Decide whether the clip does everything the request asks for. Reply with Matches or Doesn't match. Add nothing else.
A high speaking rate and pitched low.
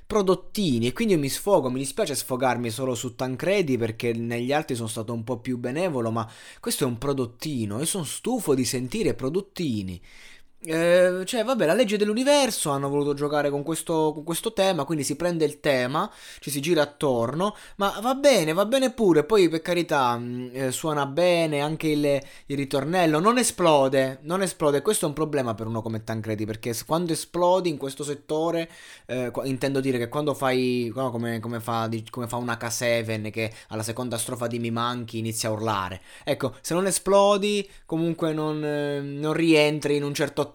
Doesn't match